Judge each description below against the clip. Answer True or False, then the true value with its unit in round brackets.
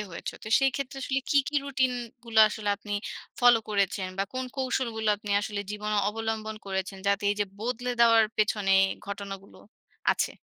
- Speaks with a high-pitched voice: True (220 Hz)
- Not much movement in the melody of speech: False (3.2 semitones)